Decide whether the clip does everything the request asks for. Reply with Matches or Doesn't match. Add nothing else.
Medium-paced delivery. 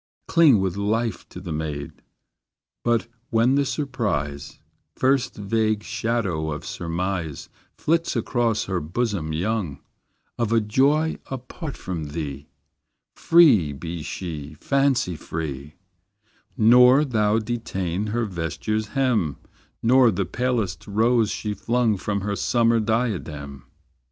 Doesn't match